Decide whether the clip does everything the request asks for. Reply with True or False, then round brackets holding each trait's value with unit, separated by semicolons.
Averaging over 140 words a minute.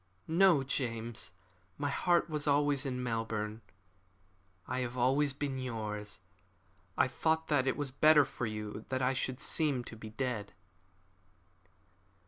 False (135 wpm)